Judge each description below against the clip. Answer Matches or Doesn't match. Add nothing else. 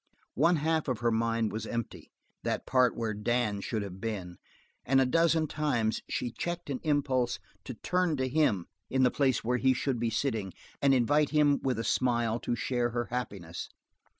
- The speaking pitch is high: Doesn't match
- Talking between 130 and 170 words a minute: Doesn't match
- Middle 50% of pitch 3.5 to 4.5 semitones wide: Matches